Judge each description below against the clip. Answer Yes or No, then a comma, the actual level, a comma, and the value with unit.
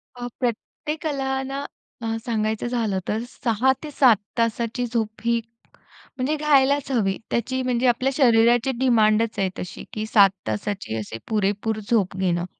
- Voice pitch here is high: Yes, high, 235 Hz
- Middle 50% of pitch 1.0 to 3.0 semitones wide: No, average, 3.6 semitones